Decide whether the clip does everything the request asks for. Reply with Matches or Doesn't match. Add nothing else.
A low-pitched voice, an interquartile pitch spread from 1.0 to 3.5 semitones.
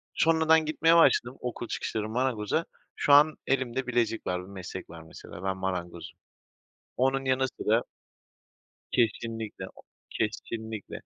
Doesn't match